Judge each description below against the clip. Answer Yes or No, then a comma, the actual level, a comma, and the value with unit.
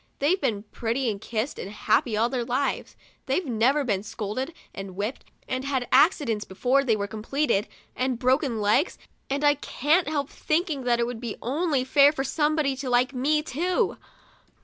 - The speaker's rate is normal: Yes, average, 175 wpm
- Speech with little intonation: No, average, 4.2 semitones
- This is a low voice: No, very high, 260 Hz